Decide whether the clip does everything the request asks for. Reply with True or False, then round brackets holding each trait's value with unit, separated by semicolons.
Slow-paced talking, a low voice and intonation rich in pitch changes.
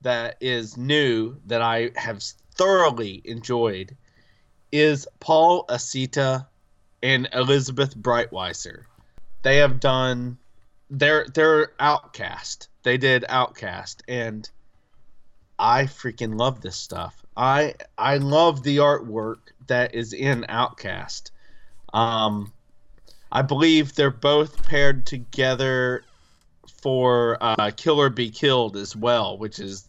False (110 wpm; 125 Hz; 3.8 semitones)